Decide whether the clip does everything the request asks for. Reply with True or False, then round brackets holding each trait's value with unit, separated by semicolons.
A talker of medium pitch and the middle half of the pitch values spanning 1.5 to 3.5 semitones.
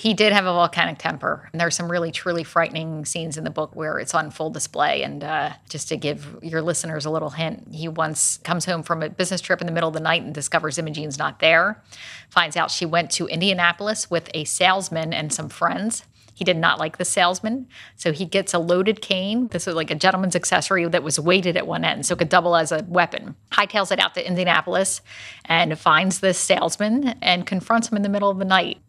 True (175 Hz; 2.8 semitones)